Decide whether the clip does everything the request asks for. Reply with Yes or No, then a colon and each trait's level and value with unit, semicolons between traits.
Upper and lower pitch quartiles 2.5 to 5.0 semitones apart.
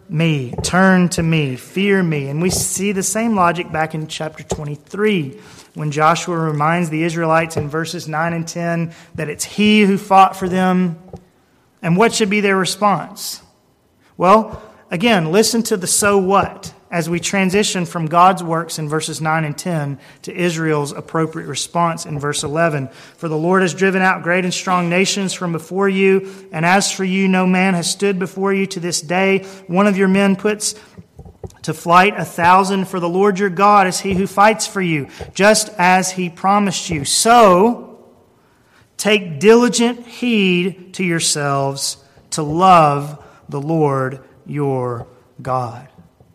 Yes: average, 3.6 semitones